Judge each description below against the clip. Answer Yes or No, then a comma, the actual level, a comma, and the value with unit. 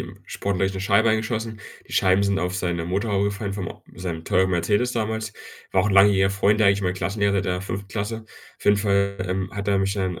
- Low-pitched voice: Yes, low, 100 Hz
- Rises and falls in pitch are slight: Yes, narrow, 1.6 semitones